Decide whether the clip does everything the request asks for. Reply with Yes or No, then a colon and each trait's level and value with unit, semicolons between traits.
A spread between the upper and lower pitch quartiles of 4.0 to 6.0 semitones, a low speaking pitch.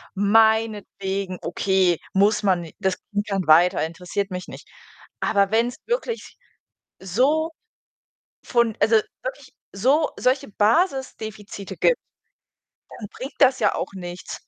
No: average, 4.9 semitones; high, 205 Hz